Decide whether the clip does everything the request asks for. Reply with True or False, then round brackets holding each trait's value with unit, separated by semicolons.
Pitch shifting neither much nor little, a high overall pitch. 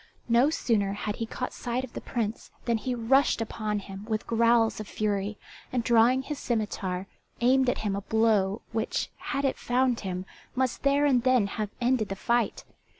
True (3.2 semitones; 230 Hz)